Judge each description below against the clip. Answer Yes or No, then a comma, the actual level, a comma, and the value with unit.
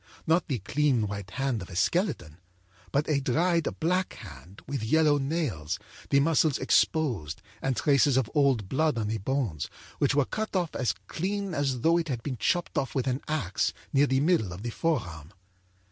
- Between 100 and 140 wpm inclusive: No, average, 185 wpm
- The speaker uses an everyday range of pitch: No, wide, 6.5 semitones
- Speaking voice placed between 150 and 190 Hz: No, low, 135 Hz